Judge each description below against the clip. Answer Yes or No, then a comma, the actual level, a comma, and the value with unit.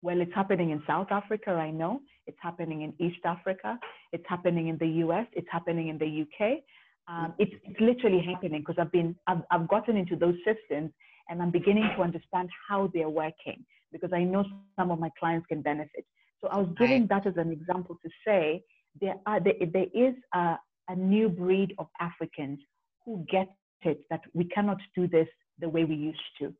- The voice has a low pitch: No, medium, 175 Hz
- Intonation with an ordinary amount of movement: Yes, average, 3.2 semitones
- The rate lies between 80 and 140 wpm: No, average, 200 wpm